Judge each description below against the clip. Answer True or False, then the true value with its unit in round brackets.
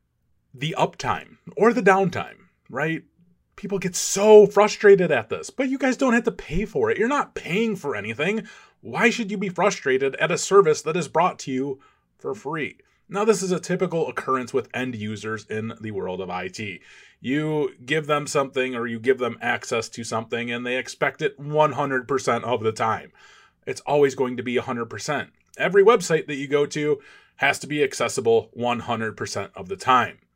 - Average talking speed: True (185 wpm)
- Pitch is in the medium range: True (150 Hz)